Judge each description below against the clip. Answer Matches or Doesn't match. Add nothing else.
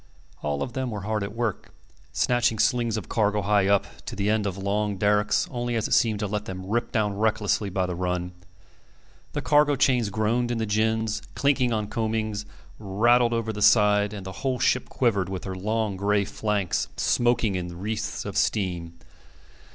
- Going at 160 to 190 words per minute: Matches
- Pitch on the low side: Matches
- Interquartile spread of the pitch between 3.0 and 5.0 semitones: Doesn't match